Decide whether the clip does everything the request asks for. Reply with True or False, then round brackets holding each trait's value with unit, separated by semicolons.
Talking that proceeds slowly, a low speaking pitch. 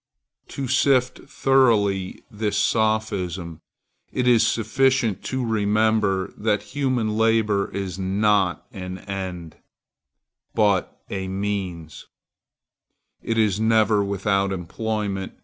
True (95 wpm; 105 Hz)